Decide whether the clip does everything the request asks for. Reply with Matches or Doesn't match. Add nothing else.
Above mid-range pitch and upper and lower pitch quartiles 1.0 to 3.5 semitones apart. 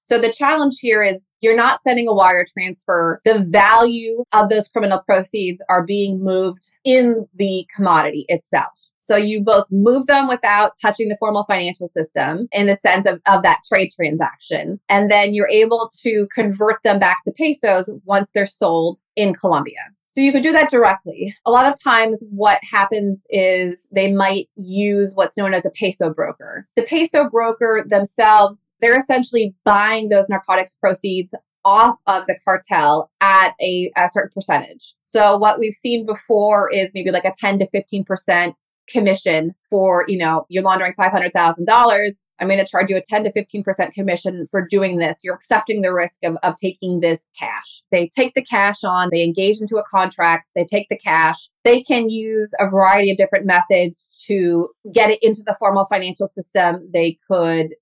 Matches